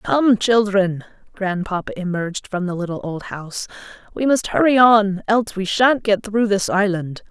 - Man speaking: No, female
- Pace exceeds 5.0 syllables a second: No, 4.7 syllables/s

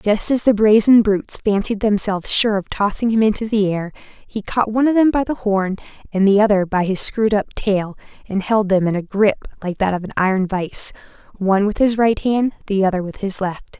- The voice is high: Yes, high, 205 Hz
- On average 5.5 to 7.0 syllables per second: Yes, 5.6 syllables/s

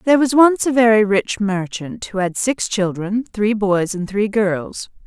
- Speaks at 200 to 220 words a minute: No, average, 190 wpm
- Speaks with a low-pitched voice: No, high, 210 Hz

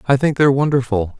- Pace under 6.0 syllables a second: No, 6.6 syllables/s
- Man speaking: Yes, male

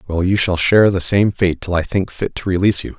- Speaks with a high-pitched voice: No, very low, 95 Hz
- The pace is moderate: No, fast, 280 wpm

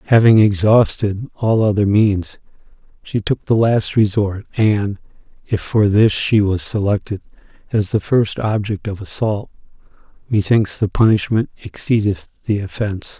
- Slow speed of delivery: Yes, slow, 130 wpm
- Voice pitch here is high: No, low, 105 Hz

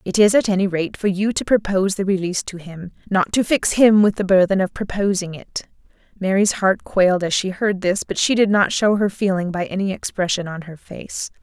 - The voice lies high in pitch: Yes, high, 195 Hz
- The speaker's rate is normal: No, fast, 220 wpm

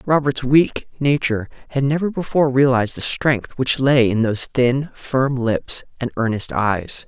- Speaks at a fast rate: No, average, 160 wpm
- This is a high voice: No, low, 130 Hz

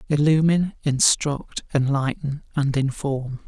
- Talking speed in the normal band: No, slow, 85 wpm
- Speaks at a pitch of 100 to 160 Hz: Yes, medium, 145 Hz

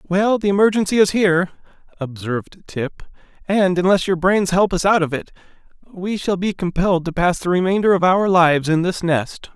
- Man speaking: Yes, male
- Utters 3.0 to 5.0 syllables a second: No, 5.2 syllables/s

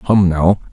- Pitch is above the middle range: No, very low, 90 Hz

